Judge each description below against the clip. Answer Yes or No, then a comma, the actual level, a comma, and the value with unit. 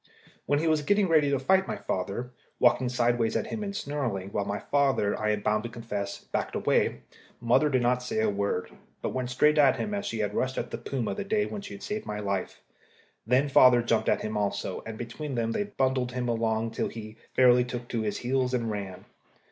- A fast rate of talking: Yes, fast, 220 wpm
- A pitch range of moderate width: Yes, average, 4.5 semitones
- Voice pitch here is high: No, low, 125 Hz